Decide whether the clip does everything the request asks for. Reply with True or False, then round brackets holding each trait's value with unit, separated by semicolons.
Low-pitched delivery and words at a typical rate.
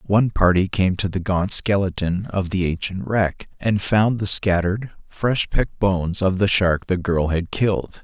True (95 Hz; 185 wpm)